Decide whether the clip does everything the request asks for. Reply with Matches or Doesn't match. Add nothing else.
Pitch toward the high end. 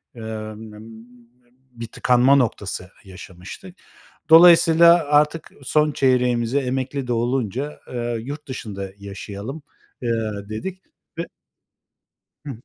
Doesn't match